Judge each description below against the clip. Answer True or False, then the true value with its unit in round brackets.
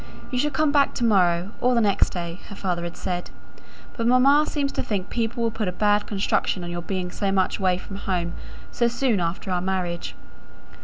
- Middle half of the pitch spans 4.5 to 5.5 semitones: True (4.8 semitones)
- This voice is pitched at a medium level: False (200 Hz)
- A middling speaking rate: False (210 wpm)